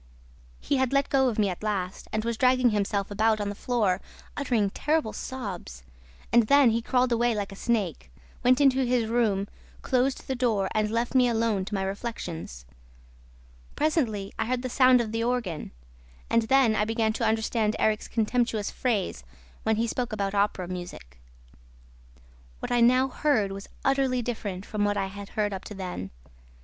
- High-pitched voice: Yes, high, 220 Hz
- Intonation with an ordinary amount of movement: Yes, average, 3.7 semitones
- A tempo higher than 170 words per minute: Yes, average, 180 wpm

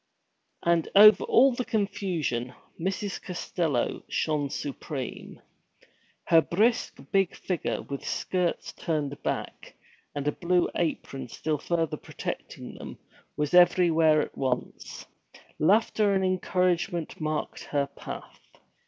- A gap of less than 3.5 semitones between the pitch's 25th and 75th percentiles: No, average, 4.2 semitones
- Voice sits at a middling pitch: Yes, medium, 170 Hz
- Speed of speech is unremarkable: No, slow, 110 wpm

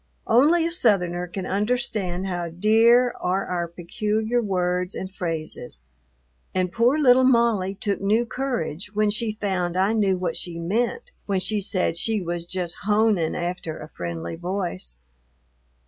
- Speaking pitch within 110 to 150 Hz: No, high, 195 Hz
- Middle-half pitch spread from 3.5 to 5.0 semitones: Yes, average, 4.1 semitones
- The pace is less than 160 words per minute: Yes, average, 145 wpm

